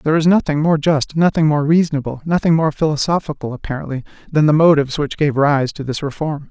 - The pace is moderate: Yes, average, 195 wpm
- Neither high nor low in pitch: Yes, medium, 150 Hz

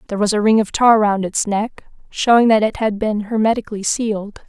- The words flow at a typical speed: No, fast, 215 wpm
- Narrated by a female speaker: Yes, female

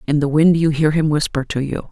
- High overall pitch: No, medium, 150 Hz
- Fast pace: Yes, fast, 280 wpm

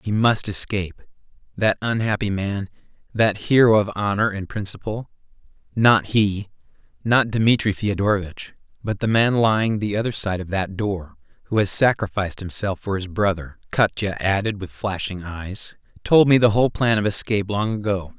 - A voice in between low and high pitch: No, low, 105 Hz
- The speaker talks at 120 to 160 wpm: Yes, average, 150 wpm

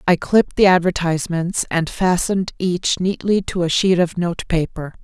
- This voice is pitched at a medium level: Yes, medium, 175 Hz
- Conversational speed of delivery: Yes, average, 155 wpm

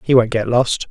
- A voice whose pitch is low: Yes, low, 120 Hz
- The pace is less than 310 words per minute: Yes, fast, 265 wpm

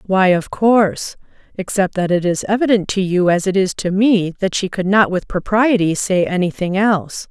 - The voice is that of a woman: Yes, female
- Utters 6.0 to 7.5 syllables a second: No, 5.0 syllables/s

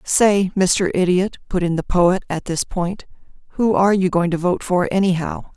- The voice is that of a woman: Yes, female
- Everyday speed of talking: Yes, average, 195 wpm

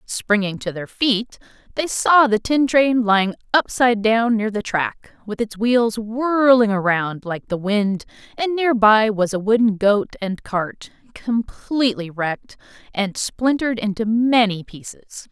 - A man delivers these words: No, female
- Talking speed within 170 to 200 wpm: No, average, 155 wpm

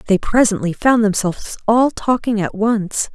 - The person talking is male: No, female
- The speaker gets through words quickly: No, average, 155 wpm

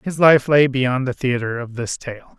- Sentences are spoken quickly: Yes, fast, 225 wpm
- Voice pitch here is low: Yes, low, 130 Hz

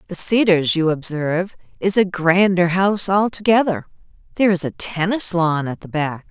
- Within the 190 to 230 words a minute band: No, average, 160 wpm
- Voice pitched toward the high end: No, medium, 180 Hz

